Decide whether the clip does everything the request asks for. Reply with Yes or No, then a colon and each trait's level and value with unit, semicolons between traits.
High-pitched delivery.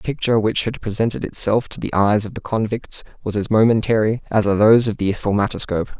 No: low, 110 Hz